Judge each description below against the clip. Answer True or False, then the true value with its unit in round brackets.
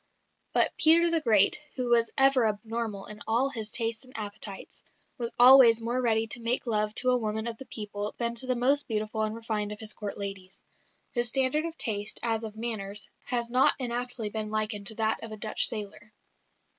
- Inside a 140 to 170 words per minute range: False (200 wpm)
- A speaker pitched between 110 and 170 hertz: False (225 Hz)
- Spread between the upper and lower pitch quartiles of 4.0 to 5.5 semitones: False (2.5 semitones)